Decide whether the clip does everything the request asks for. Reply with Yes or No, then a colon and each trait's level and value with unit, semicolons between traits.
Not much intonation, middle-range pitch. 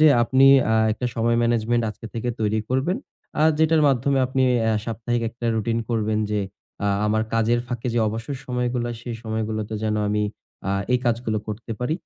No: narrow, 2.0 semitones; low, 115 Hz